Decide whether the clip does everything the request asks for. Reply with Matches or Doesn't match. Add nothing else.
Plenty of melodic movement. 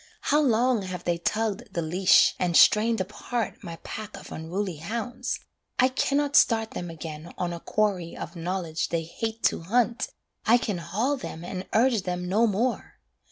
Doesn't match